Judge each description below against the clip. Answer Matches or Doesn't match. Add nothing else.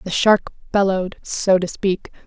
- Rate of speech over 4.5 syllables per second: Doesn't match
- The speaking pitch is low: Doesn't match